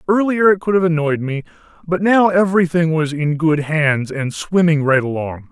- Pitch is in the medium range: Yes, medium, 165 Hz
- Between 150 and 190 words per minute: Yes, average, 185 wpm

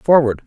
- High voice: No, low, 130 Hz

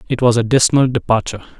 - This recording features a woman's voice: No, male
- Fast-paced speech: No, average, 190 wpm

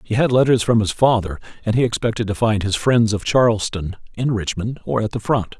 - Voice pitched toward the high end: No, low, 110 Hz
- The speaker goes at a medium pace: No, fast, 225 wpm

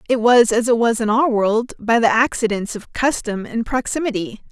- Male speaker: No, female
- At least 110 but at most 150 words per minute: No, average, 200 wpm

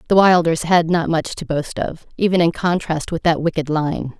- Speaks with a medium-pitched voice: Yes, medium, 165 Hz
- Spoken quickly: Yes, fast, 215 wpm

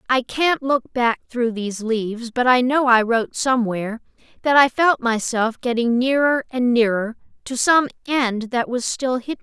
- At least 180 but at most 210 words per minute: Yes, average, 190 wpm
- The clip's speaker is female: Yes, female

